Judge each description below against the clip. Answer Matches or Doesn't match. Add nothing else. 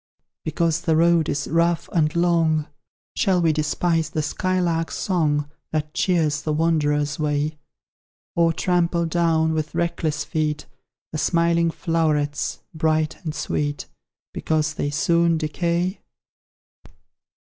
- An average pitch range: Doesn't match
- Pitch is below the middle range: Doesn't match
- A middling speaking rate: Doesn't match